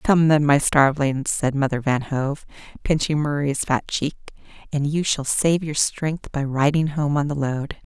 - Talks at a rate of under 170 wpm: No, average, 180 wpm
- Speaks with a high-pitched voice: No, medium, 145 Hz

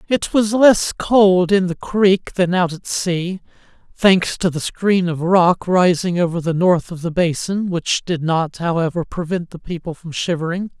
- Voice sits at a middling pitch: Yes, medium, 180 Hz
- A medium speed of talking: Yes, average, 185 wpm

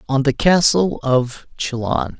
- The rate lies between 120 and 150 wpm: Yes, slow, 135 wpm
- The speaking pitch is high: No, low, 135 Hz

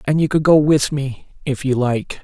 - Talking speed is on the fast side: Yes, fast, 240 wpm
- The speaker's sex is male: Yes, male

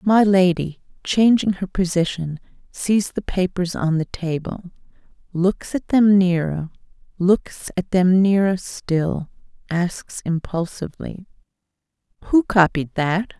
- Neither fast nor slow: No, slow, 100 wpm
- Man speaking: No, female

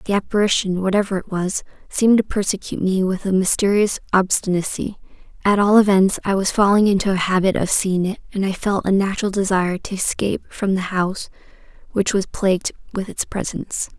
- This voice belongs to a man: No, female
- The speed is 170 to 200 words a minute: Yes, average, 180 wpm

